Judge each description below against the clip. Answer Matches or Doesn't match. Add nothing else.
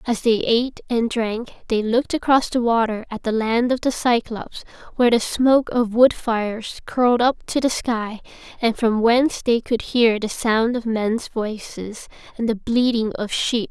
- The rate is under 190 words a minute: Doesn't match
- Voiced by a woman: Matches